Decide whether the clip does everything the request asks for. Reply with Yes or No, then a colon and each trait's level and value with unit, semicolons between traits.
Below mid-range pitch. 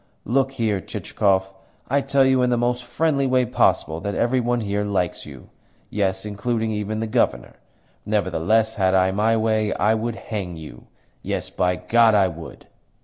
Yes: low, 110 Hz